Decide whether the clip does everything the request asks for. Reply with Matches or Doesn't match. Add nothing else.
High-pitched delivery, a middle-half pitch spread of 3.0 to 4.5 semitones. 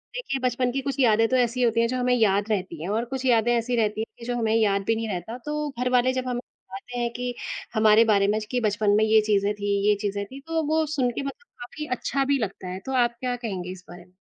Matches